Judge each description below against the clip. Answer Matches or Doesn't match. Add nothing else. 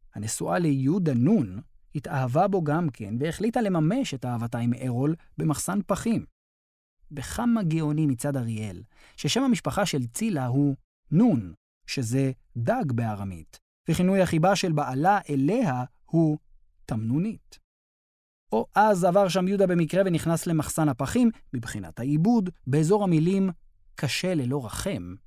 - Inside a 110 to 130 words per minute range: Matches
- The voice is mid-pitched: Matches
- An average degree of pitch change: Doesn't match